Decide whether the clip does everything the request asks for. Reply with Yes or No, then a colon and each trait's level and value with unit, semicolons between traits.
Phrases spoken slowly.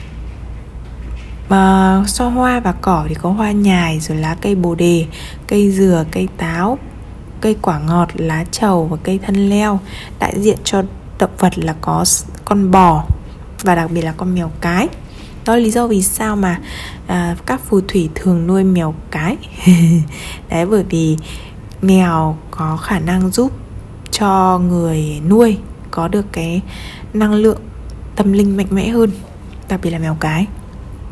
Yes: slow, 160 wpm